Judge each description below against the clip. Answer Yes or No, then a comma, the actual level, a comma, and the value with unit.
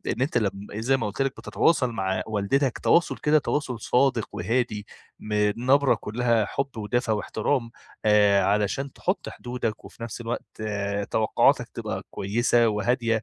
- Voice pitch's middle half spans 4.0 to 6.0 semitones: No, average, 3.3 semitones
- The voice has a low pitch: Yes, low, 115 Hz